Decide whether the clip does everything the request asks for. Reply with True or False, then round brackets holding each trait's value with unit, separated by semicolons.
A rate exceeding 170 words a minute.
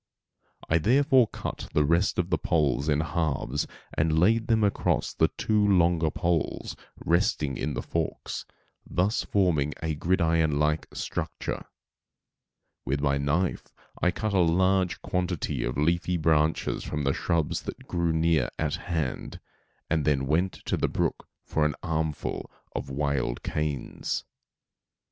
False (140 wpm)